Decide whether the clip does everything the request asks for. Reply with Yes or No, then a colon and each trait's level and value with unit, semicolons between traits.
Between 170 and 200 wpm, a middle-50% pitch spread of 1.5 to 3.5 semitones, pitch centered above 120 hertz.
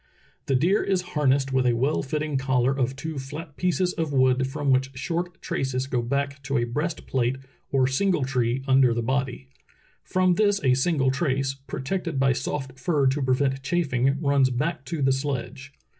Yes: average, 175 wpm; narrow, 2.6 semitones; low, 135 Hz